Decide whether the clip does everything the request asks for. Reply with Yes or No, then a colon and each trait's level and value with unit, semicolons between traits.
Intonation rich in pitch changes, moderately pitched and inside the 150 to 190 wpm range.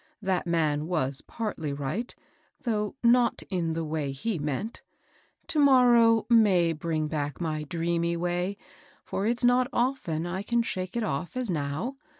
Yes: wide, 6.7 semitones; medium, 175 Hz; average, 155 wpm